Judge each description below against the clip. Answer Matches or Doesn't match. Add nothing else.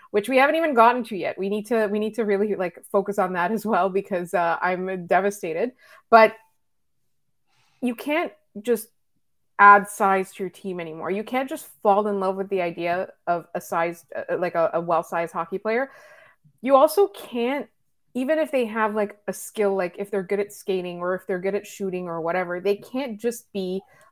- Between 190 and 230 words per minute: Matches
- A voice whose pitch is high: Matches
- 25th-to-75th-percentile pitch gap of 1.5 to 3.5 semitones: Doesn't match